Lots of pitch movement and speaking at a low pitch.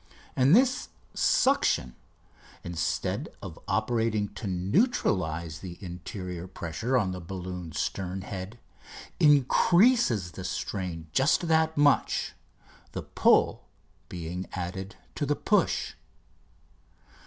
Yes: wide, 7.2 semitones; very low, 95 Hz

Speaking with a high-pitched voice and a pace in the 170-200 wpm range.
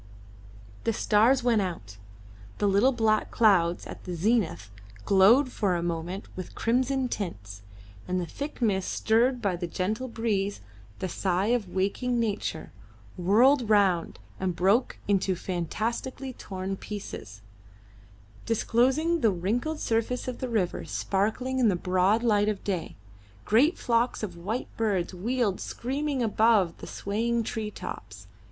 No: high, 210 Hz; average, 140 wpm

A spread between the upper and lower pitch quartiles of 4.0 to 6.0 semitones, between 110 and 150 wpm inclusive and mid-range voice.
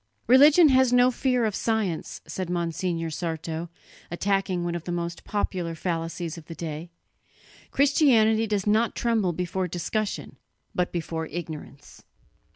Yes: average, 4.9 semitones; slow, 135 wpm; medium, 180 Hz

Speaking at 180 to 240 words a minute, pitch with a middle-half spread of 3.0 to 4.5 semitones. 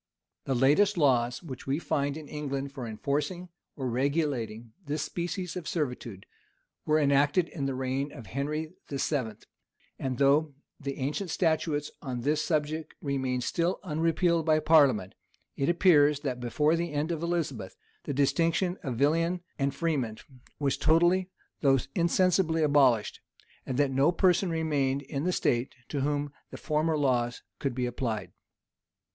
No: average, 150 wpm; average, 3.4 semitones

